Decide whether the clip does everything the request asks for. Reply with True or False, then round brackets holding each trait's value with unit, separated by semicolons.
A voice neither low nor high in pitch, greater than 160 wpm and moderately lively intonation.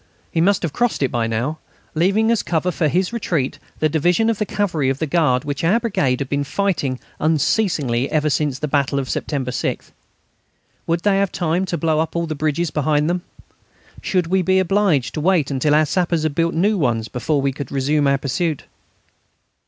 True (155 Hz; 200 wpm; 4.4 semitones)